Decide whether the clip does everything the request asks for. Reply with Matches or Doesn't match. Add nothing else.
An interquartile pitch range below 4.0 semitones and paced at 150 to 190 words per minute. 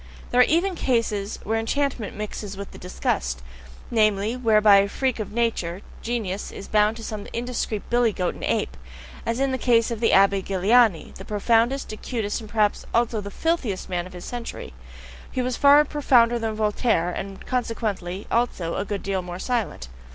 Matches